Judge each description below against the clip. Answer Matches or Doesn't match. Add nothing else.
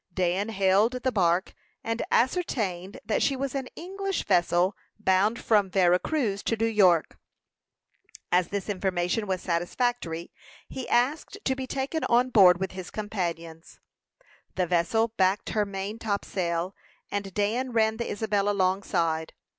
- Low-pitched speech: Doesn't match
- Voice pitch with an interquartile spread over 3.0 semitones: Matches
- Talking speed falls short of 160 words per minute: Matches